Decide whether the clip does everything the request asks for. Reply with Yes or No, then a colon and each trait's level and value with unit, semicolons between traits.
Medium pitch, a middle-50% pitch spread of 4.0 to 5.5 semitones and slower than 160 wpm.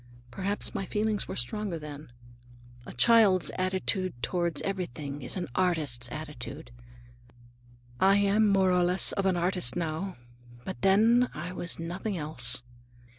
Yes: medium, 180 Hz; average, 4.5 semitones; slow, 135 wpm